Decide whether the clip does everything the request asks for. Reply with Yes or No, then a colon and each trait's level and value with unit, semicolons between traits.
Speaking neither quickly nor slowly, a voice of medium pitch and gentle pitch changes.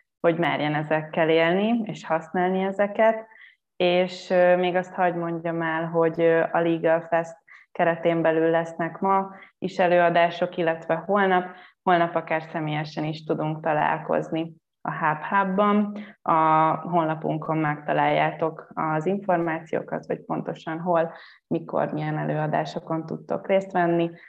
Yes: average, 120 wpm; medium, 170 Hz; narrow, 2.1 semitones